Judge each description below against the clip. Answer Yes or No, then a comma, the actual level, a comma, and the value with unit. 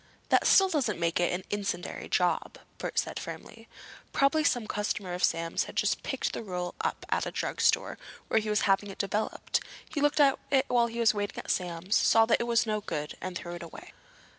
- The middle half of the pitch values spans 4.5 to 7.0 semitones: Yes, average, 4.9 semitones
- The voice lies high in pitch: Yes, high, 205 Hz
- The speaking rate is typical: No, fast, 215 wpm